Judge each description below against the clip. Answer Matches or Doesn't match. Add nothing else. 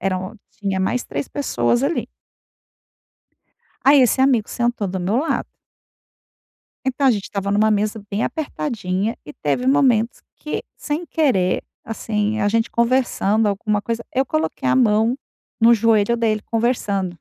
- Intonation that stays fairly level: Doesn't match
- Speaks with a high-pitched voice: Matches